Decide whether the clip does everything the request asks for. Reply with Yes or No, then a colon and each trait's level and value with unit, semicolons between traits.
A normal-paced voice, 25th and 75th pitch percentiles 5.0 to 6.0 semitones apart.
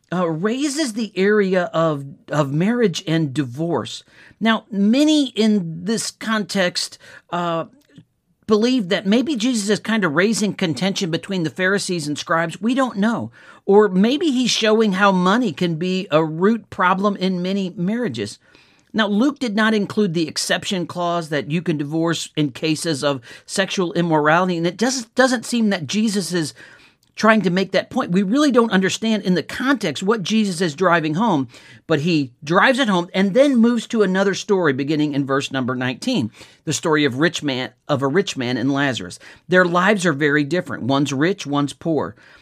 Yes: average, 175 wpm; wide, 5.4 semitones